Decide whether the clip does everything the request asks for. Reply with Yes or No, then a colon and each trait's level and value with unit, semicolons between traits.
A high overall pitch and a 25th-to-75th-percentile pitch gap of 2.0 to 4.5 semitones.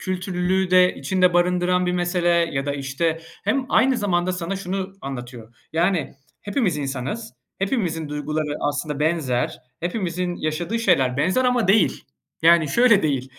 No: medium, 175 Hz; average, 4.2 semitones